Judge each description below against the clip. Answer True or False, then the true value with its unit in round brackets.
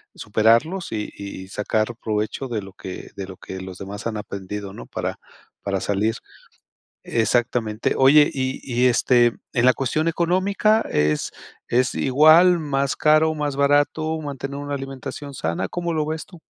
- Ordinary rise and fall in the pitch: False (6.3 semitones)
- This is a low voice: True (130 Hz)